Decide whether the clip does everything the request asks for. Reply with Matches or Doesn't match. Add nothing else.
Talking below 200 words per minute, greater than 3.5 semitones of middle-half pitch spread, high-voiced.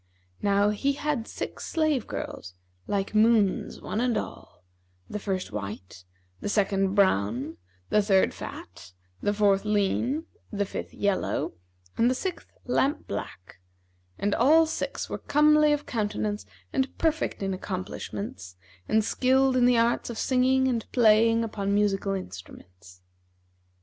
Matches